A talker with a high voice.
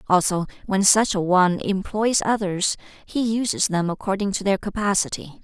Yes: high, 195 Hz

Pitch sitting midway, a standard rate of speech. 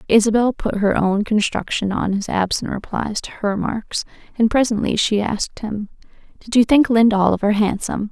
No: high, 215 Hz; average, 170 wpm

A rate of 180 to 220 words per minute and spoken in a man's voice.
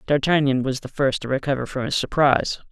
Yes: average, 200 wpm; male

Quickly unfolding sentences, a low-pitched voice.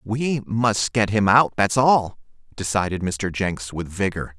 No: average, 165 wpm; low, 105 Hz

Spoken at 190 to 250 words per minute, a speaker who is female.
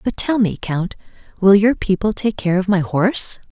Yes: fast, 205 wpm; female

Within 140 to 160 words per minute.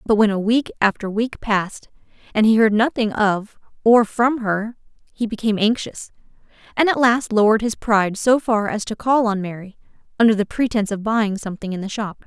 No: average, 195 wpm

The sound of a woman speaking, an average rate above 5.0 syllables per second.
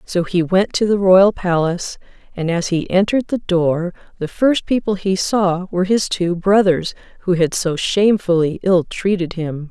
No: female; 4.6 syllables/s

